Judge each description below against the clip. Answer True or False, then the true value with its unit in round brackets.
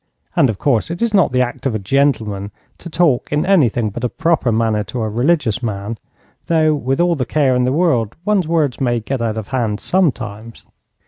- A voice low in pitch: True (125 Hz)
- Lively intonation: True (5.9 semitones)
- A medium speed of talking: False (210 wpm)